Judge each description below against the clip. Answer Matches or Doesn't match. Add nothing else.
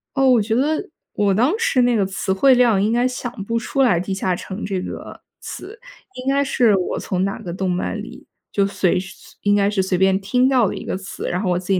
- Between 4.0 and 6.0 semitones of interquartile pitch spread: Matches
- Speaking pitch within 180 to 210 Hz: Matches